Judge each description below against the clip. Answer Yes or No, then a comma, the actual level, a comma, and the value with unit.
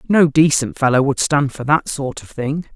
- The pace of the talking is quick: Yes, fast, 220 wpm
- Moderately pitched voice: Yes, medium, 145 Hz